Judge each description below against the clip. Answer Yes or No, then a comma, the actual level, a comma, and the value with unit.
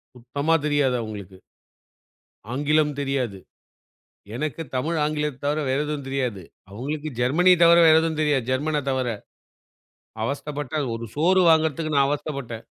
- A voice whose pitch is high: No, medium, 145 Hz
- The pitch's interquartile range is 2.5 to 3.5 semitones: Yes, average, 3.1 semitones